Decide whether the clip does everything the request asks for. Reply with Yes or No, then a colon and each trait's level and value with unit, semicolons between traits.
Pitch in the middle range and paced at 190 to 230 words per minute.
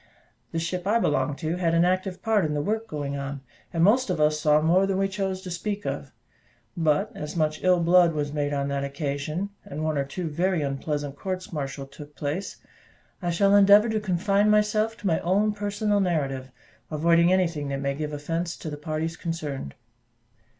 Yes: medium, 165 Hz; average, 195 wpm